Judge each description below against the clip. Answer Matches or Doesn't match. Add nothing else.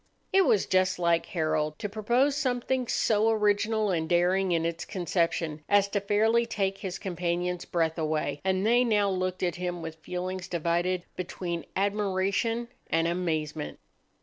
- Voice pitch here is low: Doesn't match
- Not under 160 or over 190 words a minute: Doesn't match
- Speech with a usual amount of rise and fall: Matches